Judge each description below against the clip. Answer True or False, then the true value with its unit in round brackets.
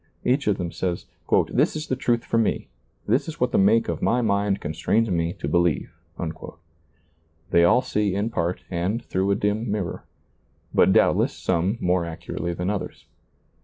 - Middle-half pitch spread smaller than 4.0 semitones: False (4.7 semitones)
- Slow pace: False (175 wpm)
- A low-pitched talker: True (100 Hz)